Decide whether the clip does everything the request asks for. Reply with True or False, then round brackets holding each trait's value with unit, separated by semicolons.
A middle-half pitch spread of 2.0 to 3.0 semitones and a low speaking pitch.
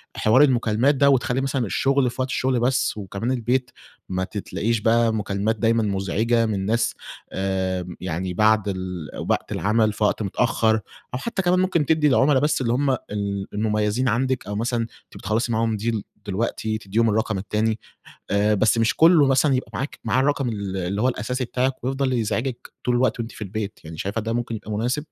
False (3.7 semitones; 115 Hz)